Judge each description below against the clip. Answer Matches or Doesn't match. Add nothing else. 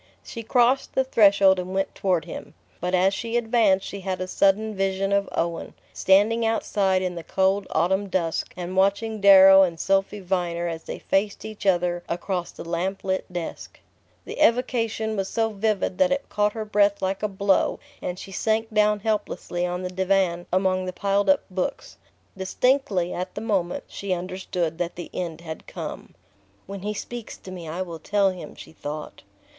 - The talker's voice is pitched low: Doesn't match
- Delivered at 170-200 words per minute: Matches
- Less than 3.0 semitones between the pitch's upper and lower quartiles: Matches